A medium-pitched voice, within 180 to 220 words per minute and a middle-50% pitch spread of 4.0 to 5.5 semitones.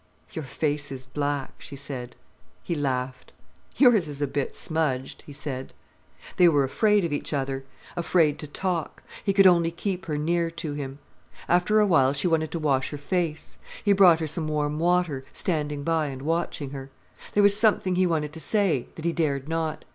No: medium, 155 Hz; average, 190 wpm; average, 3.5 semitones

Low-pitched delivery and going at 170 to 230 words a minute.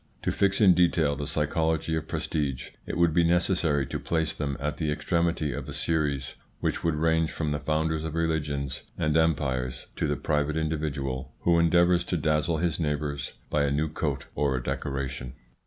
Yes: very low, 75 Hz; average, 185 wpm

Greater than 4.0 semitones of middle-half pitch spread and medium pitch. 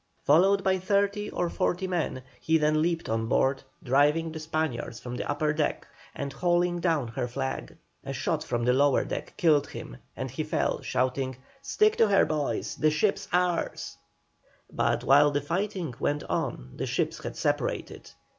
Yes: average, 4.8 semitones; medium, 155 Hz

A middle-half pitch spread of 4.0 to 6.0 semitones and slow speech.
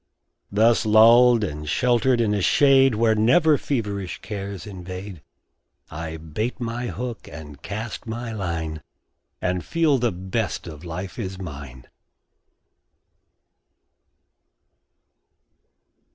Yes: average, 5.0 semitones; slow, 105 wpm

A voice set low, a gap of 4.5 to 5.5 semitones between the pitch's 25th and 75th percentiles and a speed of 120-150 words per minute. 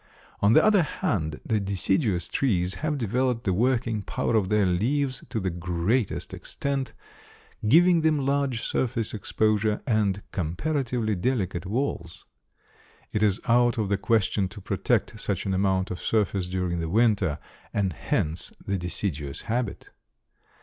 Yes: low, 105 Hz; average, 4.8 semitones; average, 145 wpm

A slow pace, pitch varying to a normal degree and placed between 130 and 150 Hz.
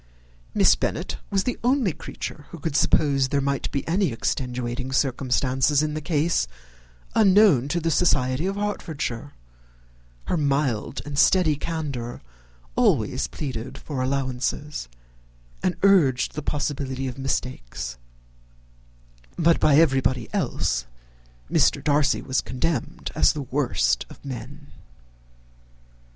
Yes: slow, 120 wpm; average, 3.6 semitones; medium, 140 Hz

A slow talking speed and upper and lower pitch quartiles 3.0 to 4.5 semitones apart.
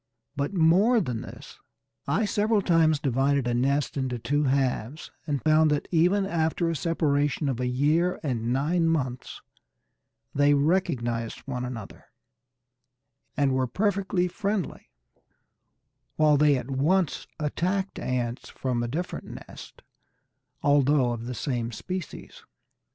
No: slow, 130 wpm; average, 4.9 semitones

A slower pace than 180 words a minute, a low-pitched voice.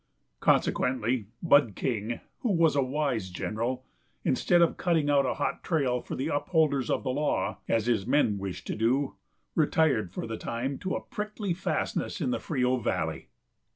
Yes: average, 170 wpm; low, 130 Hz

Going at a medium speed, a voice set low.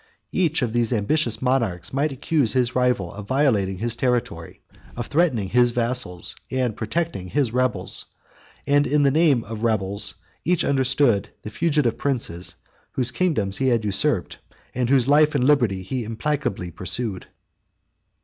Yes: average, 150 wpm; low, 125 Hz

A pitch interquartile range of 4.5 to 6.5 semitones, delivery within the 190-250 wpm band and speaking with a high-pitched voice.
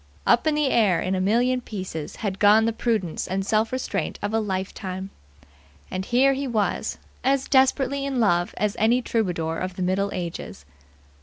No: average, 4.9 semitones; average, 175 wpm; high, 210 Hz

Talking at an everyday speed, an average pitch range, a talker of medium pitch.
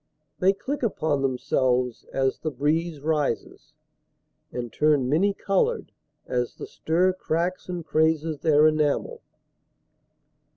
No: slow, 115 wpm; average, 4.5 semitones; medium, 155 Hz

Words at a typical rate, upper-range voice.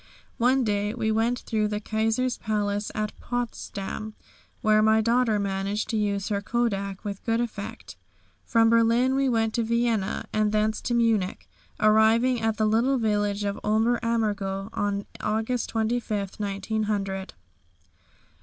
Yes: average, 145 wpm; high, 220 Hz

